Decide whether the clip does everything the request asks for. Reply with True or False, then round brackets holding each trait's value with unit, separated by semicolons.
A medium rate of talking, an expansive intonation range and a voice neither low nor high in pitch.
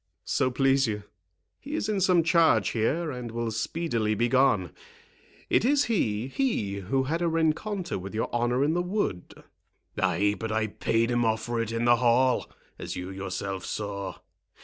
False (170 wpm; 7.1 semitones; 120 Hz)